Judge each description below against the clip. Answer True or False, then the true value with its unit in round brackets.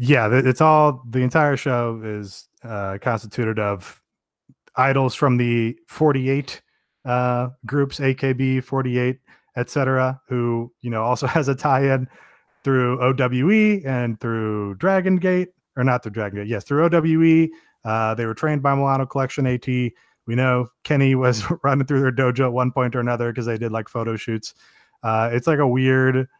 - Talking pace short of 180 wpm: True (160 wpm)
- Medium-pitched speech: False (125 Hz)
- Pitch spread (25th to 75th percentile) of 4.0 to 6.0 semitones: False (2.7 semitones)